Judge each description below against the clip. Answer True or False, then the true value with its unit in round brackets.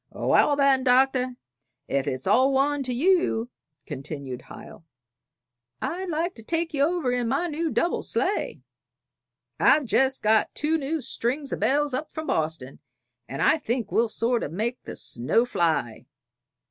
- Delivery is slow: False (155 wpm)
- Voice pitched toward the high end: True (260 Hz)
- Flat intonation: False (5.2 semitones)